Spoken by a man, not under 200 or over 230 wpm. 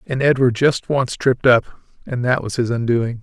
Yes: male; fast, 205 wpm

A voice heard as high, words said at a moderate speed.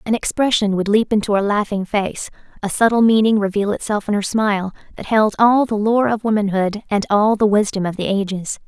No: high, 210 Hz; fast, 210 wpm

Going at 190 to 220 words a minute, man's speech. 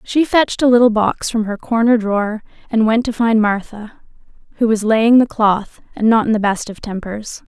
No: fast, 205 wpm; female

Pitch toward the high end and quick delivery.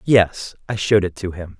No: very low, 95 Hz; fast, 225 wpm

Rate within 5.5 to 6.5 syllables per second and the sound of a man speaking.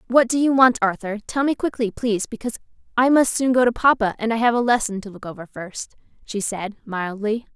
No: 5.8 syllables/s; female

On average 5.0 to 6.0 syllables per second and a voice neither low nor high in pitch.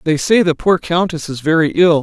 Yes: 5.2 syllables/s; medium, 165 Hz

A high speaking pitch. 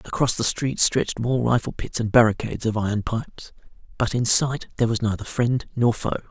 No: low, 115 Hz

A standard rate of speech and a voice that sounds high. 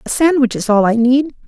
No: fast, 245 wpm; very high, 250 Hz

